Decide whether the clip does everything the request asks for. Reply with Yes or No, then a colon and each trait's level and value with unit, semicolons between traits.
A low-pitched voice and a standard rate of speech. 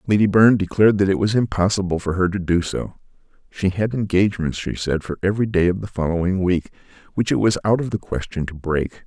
No: very low, 95 Hz; fast, 220 wpm